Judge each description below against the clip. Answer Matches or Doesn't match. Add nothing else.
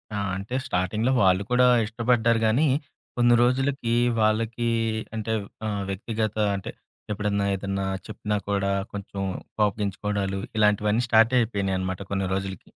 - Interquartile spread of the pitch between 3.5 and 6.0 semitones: Doesn't match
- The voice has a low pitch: Matches